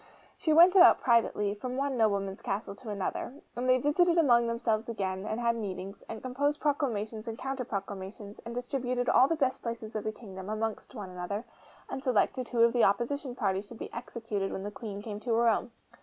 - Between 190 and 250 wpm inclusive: Yes, average, 200 wpm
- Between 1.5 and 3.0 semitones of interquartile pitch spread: No, average, 3.7 semitones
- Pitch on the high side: Yes, high, 230 Hz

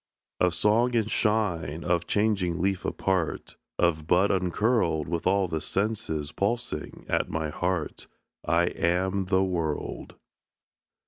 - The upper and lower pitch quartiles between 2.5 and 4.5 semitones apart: Yes, average, 3.6 semitones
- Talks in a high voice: No, very low, 90 Hz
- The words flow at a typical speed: No, slow, 125 wpm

